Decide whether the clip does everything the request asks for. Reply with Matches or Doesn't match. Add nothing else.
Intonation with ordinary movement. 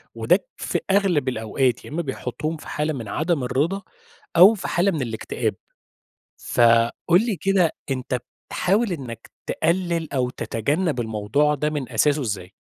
Doesn't match